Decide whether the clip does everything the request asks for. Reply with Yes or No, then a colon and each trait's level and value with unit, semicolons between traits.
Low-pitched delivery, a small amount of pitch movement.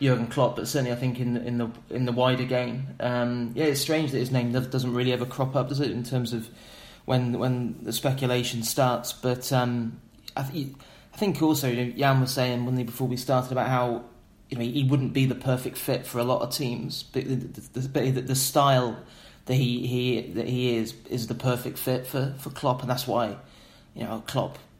Yes: low, 125 Hz; narrow, 1.5 semitones